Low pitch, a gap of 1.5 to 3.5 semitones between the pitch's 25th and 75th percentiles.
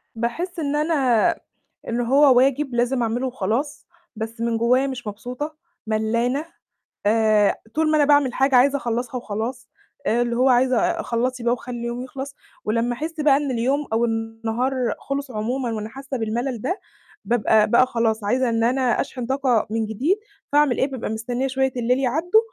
No: high, 245 Hz; average, 2.9 semitones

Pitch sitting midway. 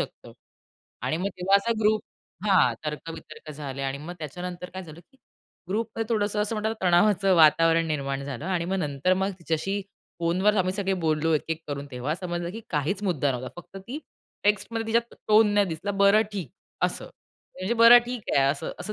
Yes: medium, 180 Hz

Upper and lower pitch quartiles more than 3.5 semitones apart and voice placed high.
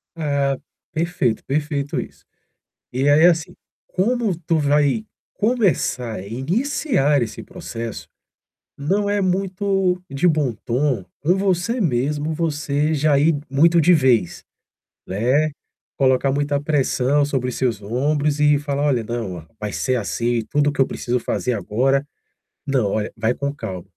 No: average, 4.6 semitones; medium, 145 Hz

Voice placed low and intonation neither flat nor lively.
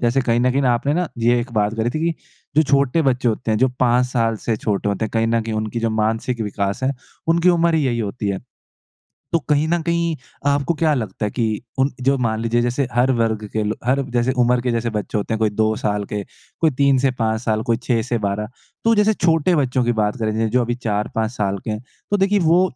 Yes: low, 120 Hz; average, 4.0 semitones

